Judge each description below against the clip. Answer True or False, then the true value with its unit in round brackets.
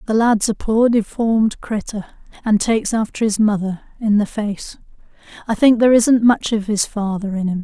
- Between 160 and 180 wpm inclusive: False (190 wpm)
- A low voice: False (215 Hz)